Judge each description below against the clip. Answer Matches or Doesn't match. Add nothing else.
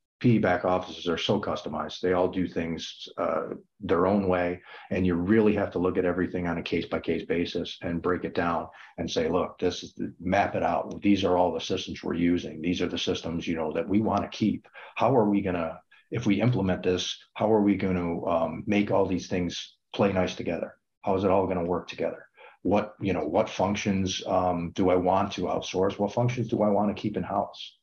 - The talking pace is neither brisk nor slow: Doesn't match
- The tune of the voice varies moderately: Doesn't match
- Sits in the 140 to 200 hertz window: Doesn't match